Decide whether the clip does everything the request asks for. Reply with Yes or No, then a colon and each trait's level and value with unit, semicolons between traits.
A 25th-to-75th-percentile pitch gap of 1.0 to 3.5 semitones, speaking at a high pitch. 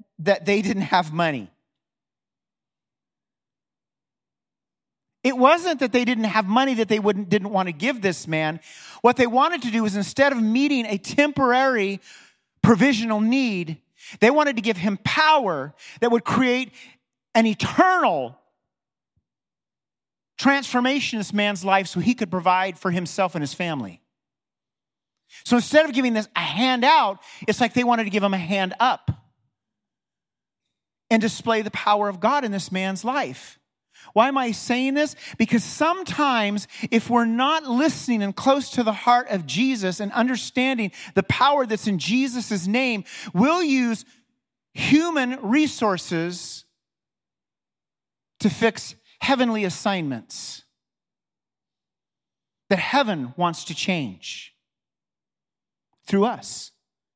No: average, 4.6 semitones; high, 225 Hz